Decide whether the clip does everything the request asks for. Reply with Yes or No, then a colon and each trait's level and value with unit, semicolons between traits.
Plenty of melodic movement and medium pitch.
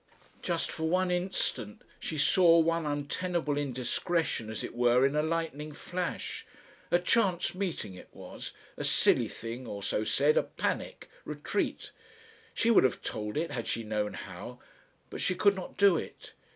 Yes: wide, 6.7 semitones; medium, 150 Hz